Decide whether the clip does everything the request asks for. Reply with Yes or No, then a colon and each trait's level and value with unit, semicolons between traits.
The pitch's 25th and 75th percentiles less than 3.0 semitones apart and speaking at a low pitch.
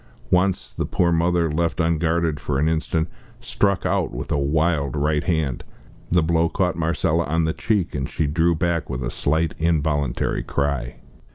Yes: narrow, 2.5 semitones; very low, 80 Hz